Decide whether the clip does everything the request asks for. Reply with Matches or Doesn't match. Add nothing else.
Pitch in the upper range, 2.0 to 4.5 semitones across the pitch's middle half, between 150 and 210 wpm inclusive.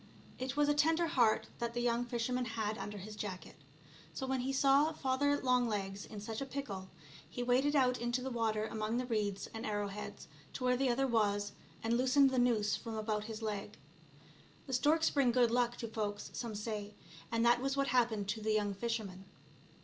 Matches